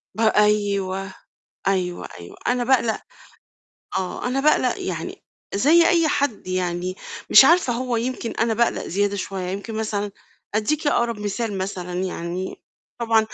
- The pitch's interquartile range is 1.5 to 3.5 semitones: No, average, 4.2 semitones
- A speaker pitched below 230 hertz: Yes, high, 210 Hz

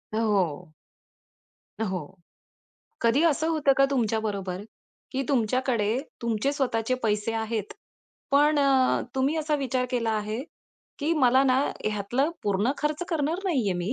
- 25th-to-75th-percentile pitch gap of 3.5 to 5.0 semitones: Yes, average, 4.7 semitones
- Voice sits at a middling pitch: No, high, 245 Hz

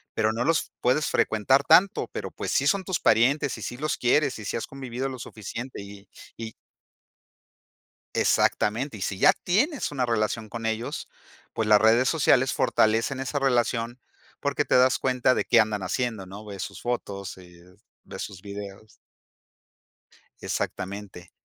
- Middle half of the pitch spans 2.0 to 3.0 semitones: No, average, 4.1 semitones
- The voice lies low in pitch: Yes, low, 115 Hz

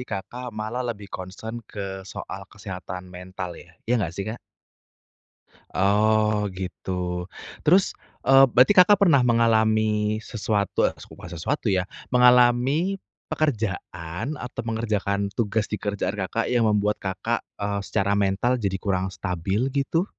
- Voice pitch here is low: Yes, low, 105 Hz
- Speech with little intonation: No, average, 4.2 semitones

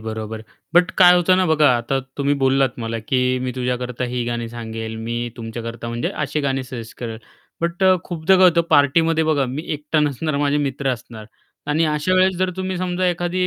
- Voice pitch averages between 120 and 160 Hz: Yes, medium, 140 Hz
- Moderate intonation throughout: No, wide, 5.9 semitones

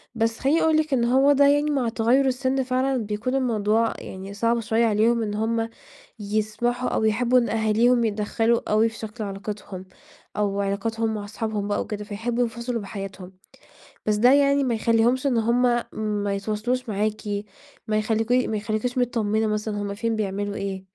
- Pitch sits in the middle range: No, high, 225 Hz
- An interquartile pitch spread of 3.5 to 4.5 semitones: No, average, 2.8 semitones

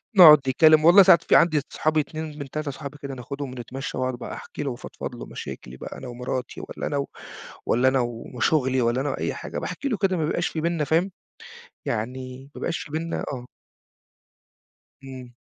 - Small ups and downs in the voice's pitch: No, average, 3.6 semitones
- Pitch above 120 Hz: Yes, medium, 140 Hz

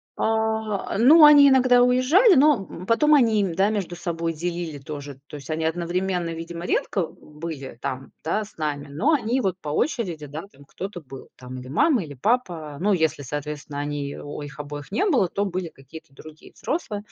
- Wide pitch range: Yes, wide, 6.9 semitones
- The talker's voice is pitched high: No, medium, 170 Hz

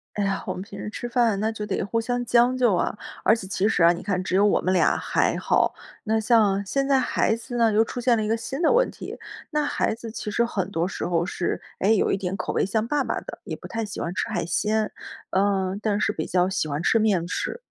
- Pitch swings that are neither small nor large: Yes, average, 3.5 semitones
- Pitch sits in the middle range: No, high, 215 Hz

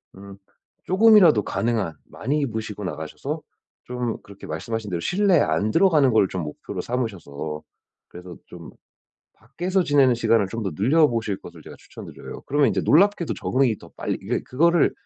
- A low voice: Yes, low, 115 Hz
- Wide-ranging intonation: Yes, wide, 7.3 semitones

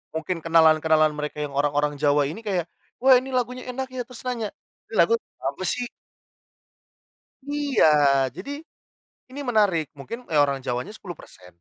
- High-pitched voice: No, medium, 165 Hz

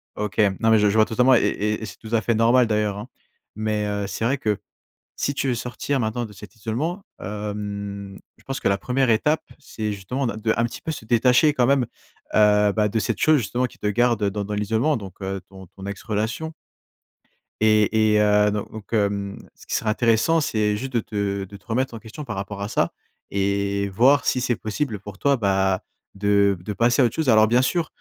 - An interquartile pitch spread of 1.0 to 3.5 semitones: Yes, average, 3.1 semitones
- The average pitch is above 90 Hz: Yes, low, 110 Hz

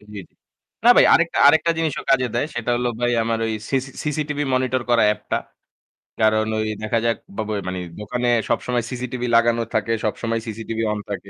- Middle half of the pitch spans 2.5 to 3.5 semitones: Yes, average, 2.9 semitones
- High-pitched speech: No, low, 120 Hz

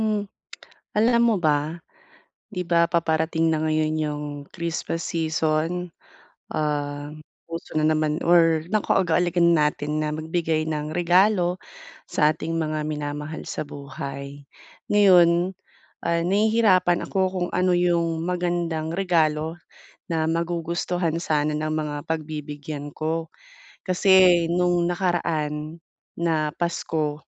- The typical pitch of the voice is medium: Yes, medium, 165 Hz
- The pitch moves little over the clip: Yes, narrow, 2.3 semitones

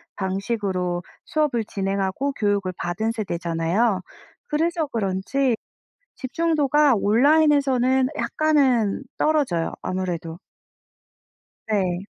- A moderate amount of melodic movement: No, wide, 6.8 semitones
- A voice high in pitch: Yes, high, 225 Hz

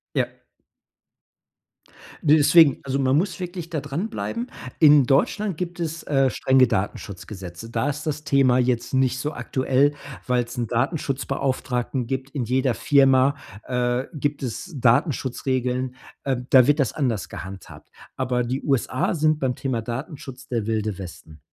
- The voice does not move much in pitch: No, average, 3.0 semitones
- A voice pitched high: No, low, 130 Hz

